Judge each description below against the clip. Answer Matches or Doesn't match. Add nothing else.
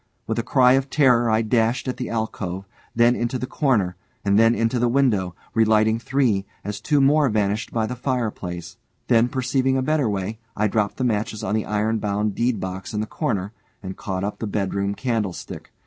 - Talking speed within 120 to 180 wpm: Doesn't match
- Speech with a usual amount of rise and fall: Matches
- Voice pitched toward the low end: Matches